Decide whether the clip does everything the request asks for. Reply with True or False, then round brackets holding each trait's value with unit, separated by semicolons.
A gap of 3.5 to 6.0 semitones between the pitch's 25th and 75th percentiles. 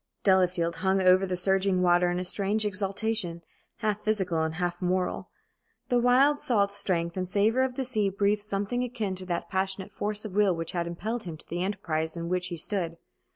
False (3.0 semitones)